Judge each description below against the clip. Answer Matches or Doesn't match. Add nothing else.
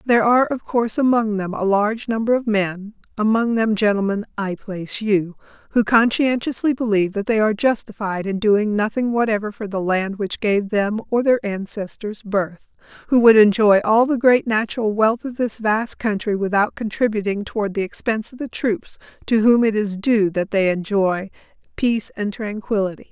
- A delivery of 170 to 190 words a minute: Matches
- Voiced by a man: Doesn't match